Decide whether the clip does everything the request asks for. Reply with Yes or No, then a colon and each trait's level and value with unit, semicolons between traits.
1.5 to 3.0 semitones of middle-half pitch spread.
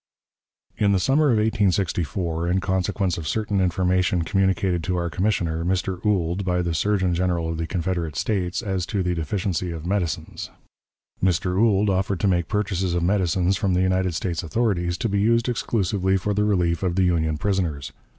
Yes: narrow, 2.4 semitones